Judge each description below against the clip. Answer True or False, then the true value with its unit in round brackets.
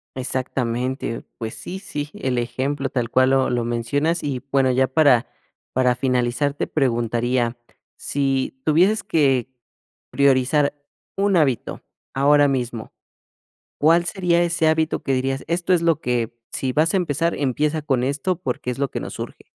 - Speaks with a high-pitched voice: False (135 Hz)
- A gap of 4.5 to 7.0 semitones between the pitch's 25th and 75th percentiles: False (3.7 semitones)